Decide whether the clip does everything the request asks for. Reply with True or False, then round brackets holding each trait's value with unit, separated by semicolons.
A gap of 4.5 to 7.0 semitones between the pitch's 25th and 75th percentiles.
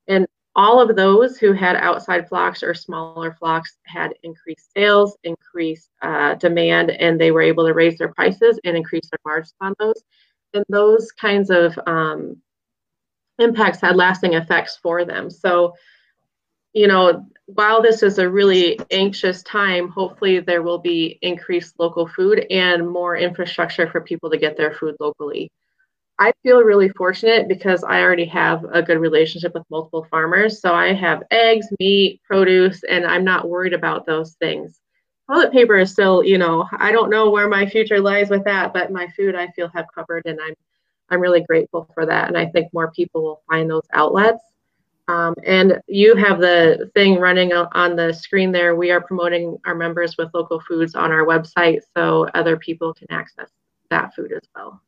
False (2.9 semitones)